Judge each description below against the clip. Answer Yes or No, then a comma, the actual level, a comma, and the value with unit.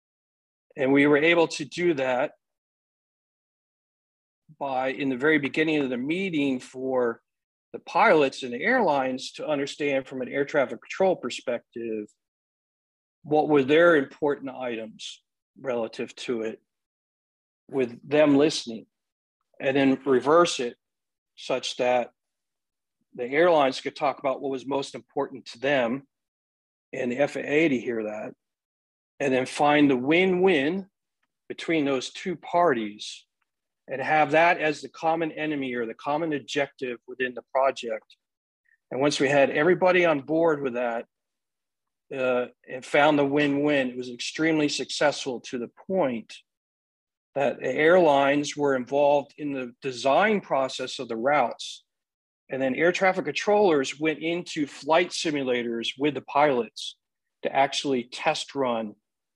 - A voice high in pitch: No, medium, 140 Hz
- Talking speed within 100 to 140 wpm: Yes, slow, 135 wpm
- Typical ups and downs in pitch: Yes, average, 3.4 semitones